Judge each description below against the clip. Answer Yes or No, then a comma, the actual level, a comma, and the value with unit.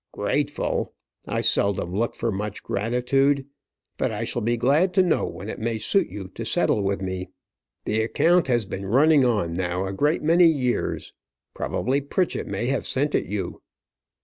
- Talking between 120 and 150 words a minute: No, average, 175 wpm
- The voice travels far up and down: Yes, wide, 6.4 semitones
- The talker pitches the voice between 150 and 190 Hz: No, low, 120 Hz